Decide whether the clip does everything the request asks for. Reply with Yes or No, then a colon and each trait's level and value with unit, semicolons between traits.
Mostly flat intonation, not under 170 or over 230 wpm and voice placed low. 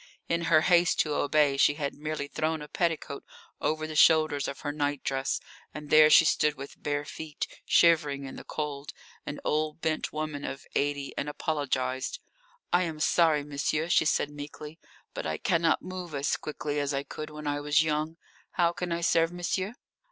No: narrow, 1.8 semitones; average, 180 wpm; medium, 150 Hz